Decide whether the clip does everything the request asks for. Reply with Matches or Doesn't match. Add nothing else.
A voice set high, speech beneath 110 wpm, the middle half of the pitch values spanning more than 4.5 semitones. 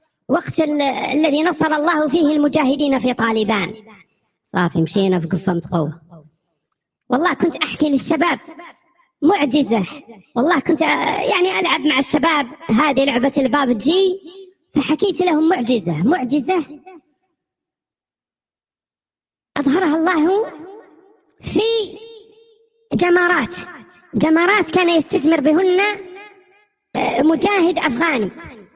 Matches